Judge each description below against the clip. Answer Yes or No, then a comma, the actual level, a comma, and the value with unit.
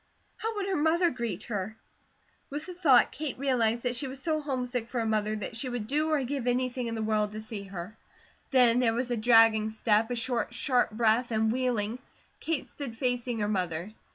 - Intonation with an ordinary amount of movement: Yes, average, 3.1 semitones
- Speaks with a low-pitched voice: No, high, 240 Hz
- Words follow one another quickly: Yes, fast, 210 wpm